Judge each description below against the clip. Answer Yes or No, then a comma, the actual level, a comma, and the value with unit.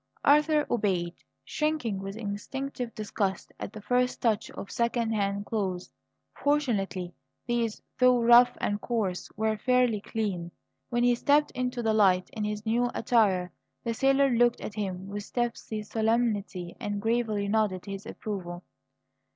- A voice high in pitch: Yes, high, 220 Hz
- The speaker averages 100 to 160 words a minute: Yes, average, 145 wpm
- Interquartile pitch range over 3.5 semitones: No, average, 3.2 semitones